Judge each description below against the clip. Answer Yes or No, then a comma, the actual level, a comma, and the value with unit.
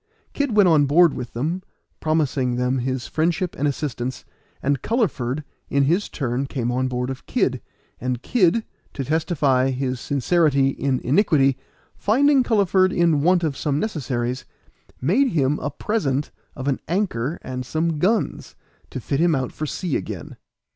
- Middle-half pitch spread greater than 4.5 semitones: Yes, average, 5.1 semitones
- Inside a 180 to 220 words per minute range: No, average, 160 wpm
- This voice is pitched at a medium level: Yes, medium, 145 Hz